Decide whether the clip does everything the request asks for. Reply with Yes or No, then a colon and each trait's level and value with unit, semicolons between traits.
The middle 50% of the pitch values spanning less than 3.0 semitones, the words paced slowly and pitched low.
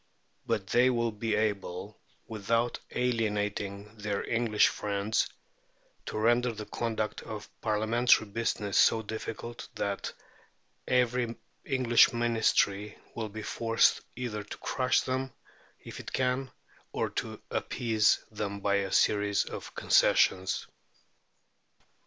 Yes: narrow, 2.4 semitones; slow, 115 wpm; low, 110 Hz